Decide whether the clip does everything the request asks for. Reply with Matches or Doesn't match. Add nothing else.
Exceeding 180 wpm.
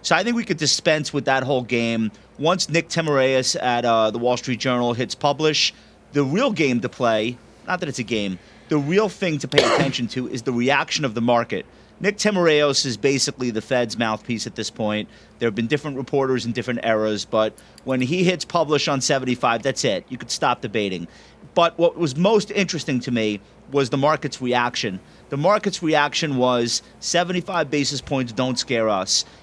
Matches